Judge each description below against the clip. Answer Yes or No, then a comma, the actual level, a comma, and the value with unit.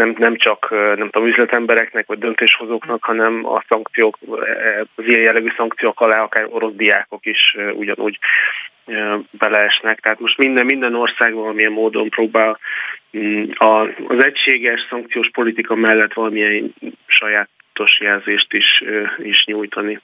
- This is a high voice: No, low, 110 Hz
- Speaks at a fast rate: No, average, 125 wpm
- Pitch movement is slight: Yes, narrow, 1.2 semitones